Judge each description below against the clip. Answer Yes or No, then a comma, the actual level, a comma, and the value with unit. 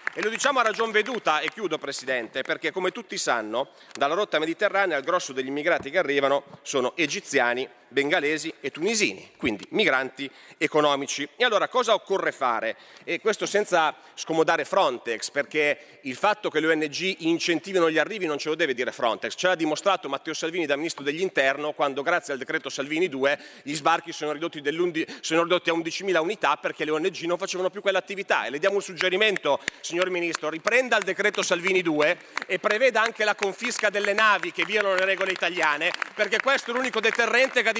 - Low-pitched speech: No, medium, 170 Hz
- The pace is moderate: No, fast, 185 wpm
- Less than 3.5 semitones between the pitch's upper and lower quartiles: No, average, 4.8 semitones